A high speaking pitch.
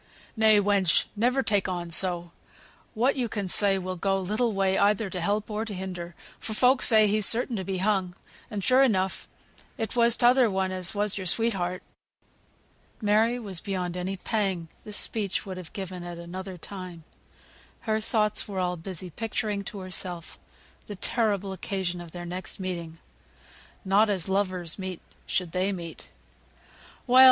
Yes: high, 195 Hz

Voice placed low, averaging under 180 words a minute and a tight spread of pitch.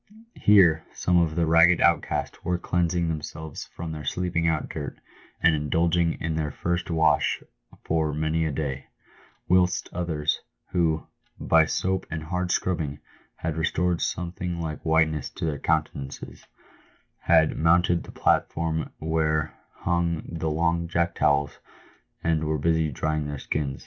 Yes: very low, 80 Hz; average, 145 wpm; narrow, 1.8 semitones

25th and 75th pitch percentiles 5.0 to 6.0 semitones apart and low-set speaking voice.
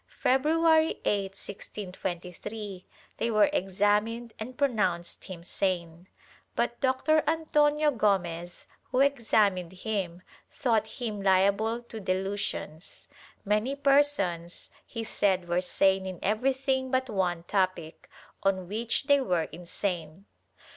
No: wide, 5.6 semitones; high, 205 Hz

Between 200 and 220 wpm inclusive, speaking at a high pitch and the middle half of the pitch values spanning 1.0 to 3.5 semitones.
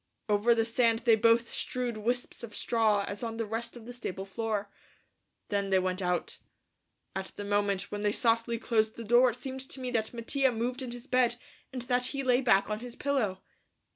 Yes: fast, 205 wpm; high, 230 Hz; average, 3.0 semitones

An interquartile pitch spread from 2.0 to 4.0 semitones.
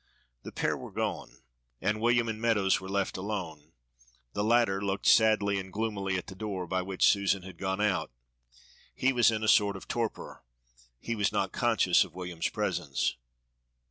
Yes: narrow, 2.5 semitones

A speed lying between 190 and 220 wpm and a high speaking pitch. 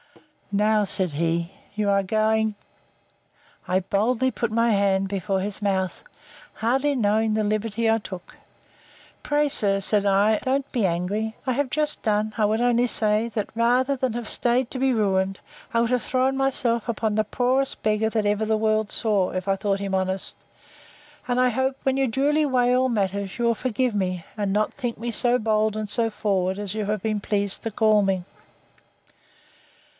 No: average, 180 wpm; high, 215 Hz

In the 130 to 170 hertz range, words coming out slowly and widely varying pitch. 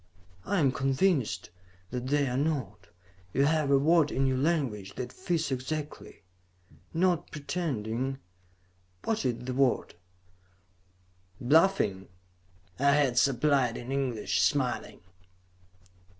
No: low, 135 Hz; slow, 110 wpm; average, 3.6 semitones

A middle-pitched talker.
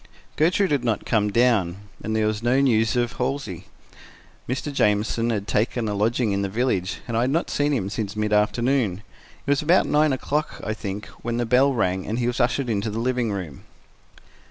No: low, 115 Hz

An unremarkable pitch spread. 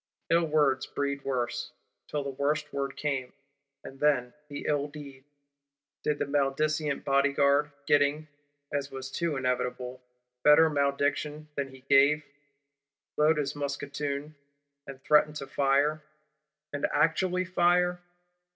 No: narrow, 1.7 semitones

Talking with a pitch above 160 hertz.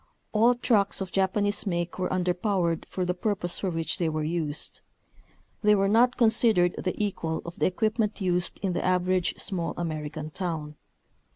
Yes: medium, 185 Hz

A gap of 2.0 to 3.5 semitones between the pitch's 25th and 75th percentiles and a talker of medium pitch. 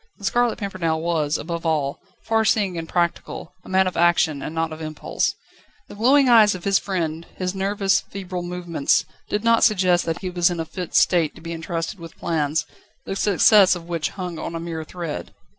Yes: average, 3.0 semitones; medium, 175 Hz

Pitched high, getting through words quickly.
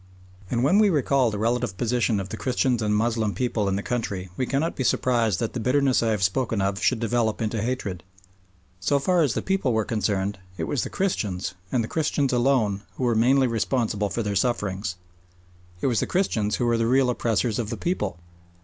No: low, 115 Hz; fast, 210 wpm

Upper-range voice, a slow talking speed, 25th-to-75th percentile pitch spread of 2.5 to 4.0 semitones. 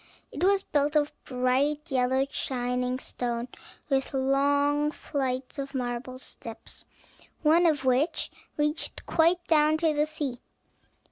Yes: very high, 280 Hz; slow, 125 wpm; average, 2.9 semitones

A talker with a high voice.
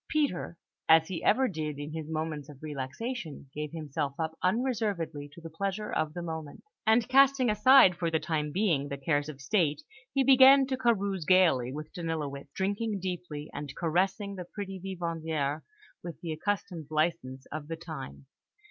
No: medium, 165 Hz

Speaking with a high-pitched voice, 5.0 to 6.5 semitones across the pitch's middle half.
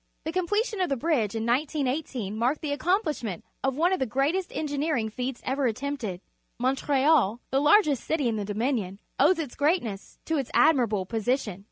Yes: very high, 270 Hz; wide, 5.4 semitones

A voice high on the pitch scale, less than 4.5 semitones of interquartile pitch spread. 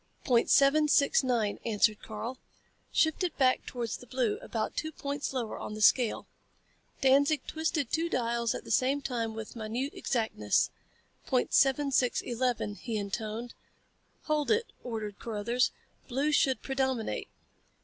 Yes: very high, 250 Hz; average, 3.8 semitones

